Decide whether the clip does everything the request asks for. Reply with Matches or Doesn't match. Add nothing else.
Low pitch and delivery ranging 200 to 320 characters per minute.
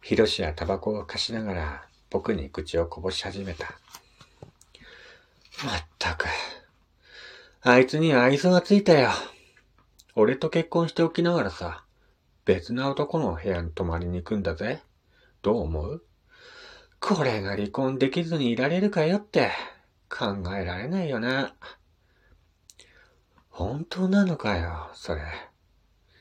Matches